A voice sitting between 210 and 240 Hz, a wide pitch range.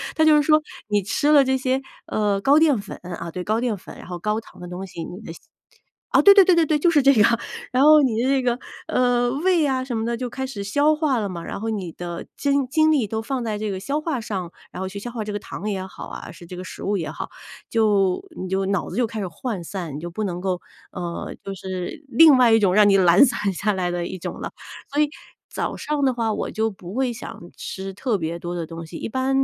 Yes: high, 215 Hz; wide, 6.0 semitones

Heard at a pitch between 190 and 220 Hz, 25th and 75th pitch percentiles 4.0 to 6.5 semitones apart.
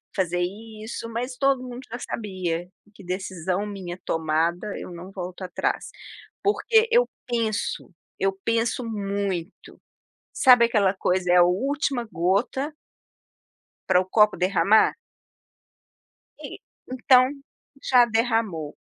Yes: high, 205 Hz; average, 4.8 semitones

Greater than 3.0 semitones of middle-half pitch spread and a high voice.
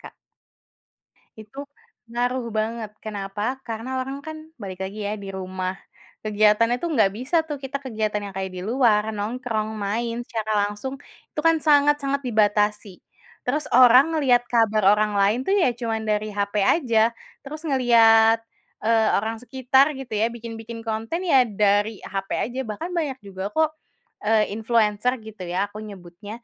Yes: average, 3.5 semitones; high, 225 Hz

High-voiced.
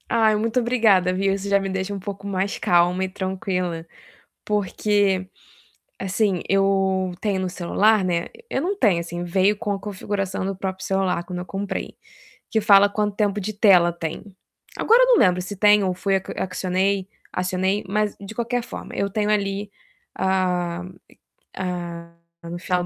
Yes: high, 195 Hz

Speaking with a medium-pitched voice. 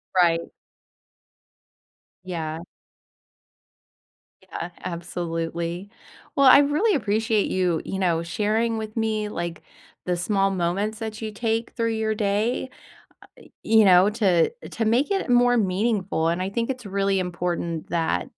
No: high, 200 Hz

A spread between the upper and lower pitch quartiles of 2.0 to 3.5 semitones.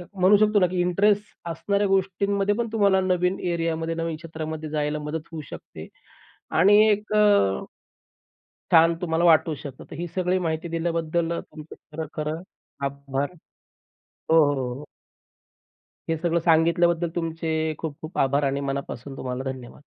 Yes: average, 2.9 semitones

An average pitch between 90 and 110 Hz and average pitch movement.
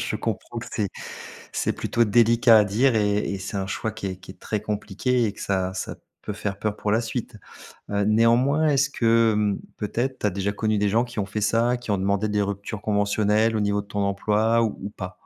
No: low, 105 Hz; narrow, 2.2 semitones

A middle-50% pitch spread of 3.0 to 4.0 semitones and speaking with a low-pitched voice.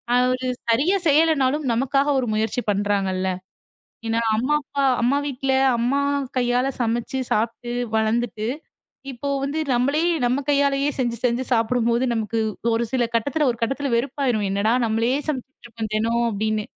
No: average, 3.3 semitones; high, 240 Hz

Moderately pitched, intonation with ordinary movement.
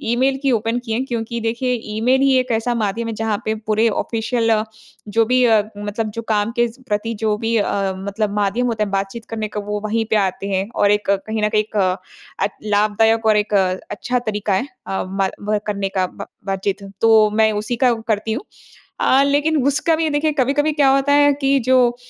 No: high, 225 Hz; average, 3.2 semitones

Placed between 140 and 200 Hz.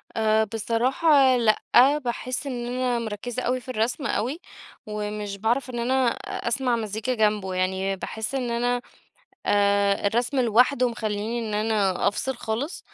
No: high, 230 Hz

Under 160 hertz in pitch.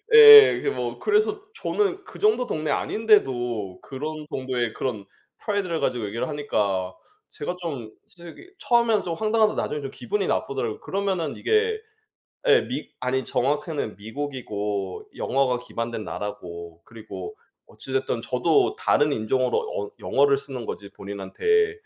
Yes: medium, 140 Hz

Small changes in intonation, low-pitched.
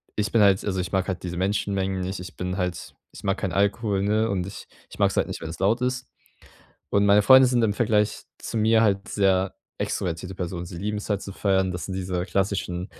Yes: narrow, 2.2 semitones; very low, 95 Hz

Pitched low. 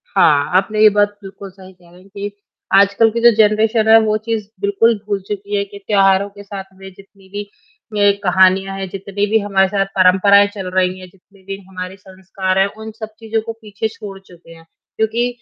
No: high, 200 Hz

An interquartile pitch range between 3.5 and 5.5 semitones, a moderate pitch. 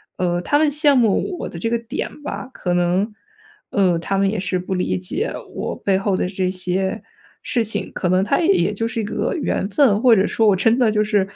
No: average, 3.9 semitones; high, 205 Hz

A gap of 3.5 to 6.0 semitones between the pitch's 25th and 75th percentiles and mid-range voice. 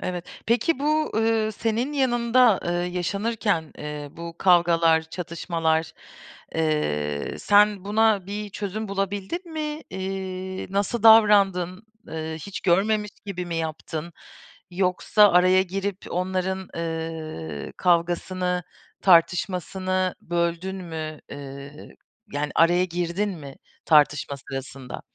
Yes: average, 3.8 semitones; medium, 180 Hz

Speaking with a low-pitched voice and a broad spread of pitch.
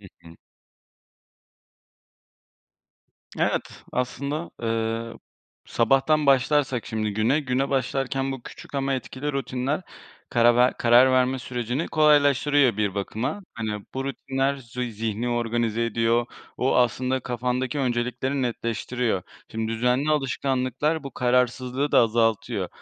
No: low, 125 Hz; narrow, 2.6 semitones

